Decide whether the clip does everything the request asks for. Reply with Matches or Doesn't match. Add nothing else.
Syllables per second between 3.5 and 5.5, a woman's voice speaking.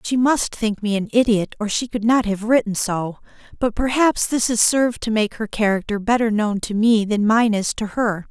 Matches